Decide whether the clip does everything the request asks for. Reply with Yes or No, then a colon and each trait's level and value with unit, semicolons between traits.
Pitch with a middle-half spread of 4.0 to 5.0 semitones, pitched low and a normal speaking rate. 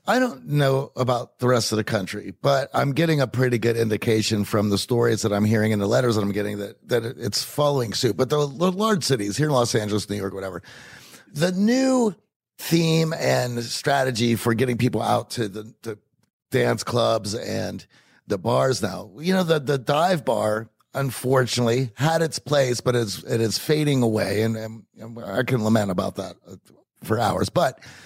Yes: average, 4.4 semitones; low, 120 Hz; average, 190 wpm